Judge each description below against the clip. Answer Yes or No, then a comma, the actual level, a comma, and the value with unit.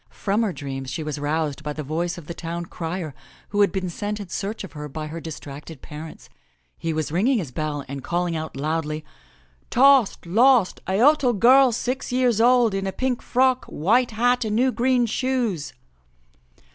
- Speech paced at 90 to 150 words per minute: No, average, 185 wpm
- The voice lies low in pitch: No, medium, 185 Hz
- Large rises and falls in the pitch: Yes, wide, 7.6 semitones